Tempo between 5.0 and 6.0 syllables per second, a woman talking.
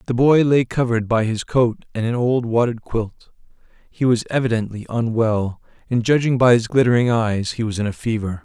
No: 5.2 syllables/s; male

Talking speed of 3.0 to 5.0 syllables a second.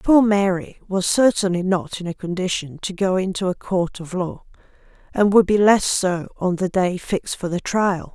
Yes: 4.7 syllables/s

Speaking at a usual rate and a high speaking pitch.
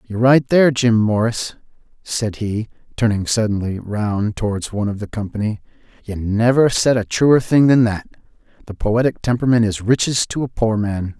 No: average, 170 wpm; low, 110 Hz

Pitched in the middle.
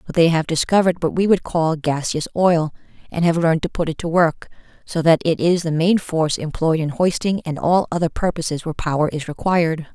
Yes: medium, 165 Hz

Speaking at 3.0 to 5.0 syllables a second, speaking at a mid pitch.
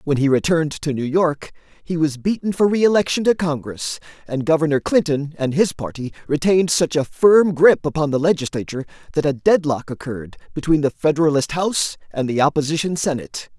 No: 5.7 syllables/s; medium, 155 Hz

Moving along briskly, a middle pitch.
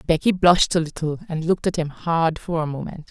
Yes: fast, 230 wpm; medium, 165 Hz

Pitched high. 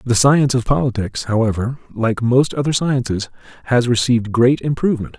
No: low, 125 Hz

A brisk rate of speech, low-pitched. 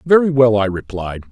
No: average, 185 wpm; low, 120 Hz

